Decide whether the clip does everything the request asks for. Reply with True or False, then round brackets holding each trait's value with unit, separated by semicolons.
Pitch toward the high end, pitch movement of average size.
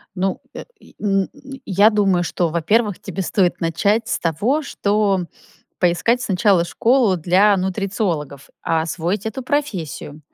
True (195 Hz; 3.5 semitones)